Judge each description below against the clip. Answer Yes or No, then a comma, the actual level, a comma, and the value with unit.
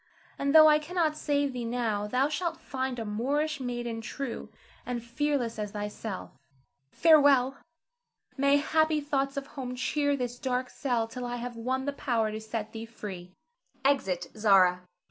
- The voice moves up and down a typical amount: Yes, average, 4.0 semitones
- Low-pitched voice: No, very high, 250 Hz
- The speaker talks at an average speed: Yes, average, 160 wpm